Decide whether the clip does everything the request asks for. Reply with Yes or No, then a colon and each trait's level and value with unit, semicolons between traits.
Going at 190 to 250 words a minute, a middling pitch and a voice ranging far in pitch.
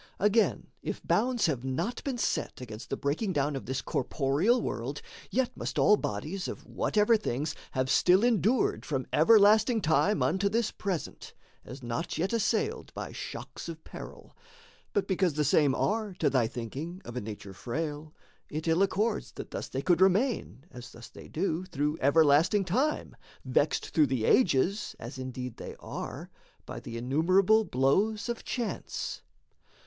No: average, 160 wpm; medium, 165 Hz; wide, 7.7 semitones